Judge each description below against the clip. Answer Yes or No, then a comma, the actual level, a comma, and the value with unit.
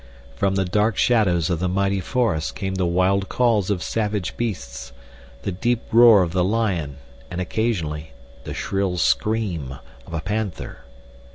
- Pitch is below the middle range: Yes, very low, 95 Hz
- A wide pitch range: No, average, 4.5 semitones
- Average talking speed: Yes, average, 150 wpm